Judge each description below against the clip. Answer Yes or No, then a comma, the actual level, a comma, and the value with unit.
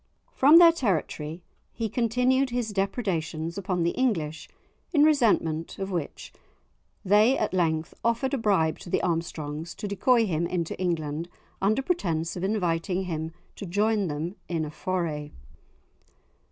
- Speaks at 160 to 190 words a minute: No, average, 140 wpm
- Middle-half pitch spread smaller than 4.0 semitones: No, wide, 5.5 semitones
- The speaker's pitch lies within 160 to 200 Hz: Yes, medium, 185 Hz